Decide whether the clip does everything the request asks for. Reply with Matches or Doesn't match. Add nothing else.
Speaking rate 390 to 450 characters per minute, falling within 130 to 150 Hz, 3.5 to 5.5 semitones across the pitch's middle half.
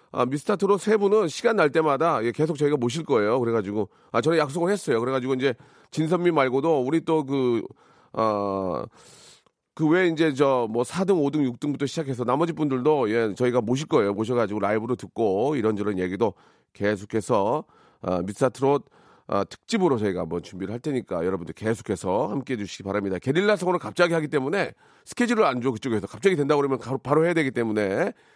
Doesn't match